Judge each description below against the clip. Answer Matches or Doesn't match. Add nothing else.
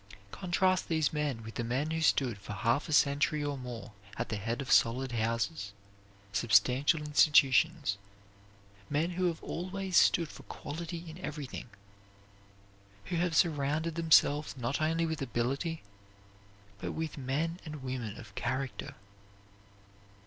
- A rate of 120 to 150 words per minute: Matches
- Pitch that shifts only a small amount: Doesn't match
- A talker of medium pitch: Matches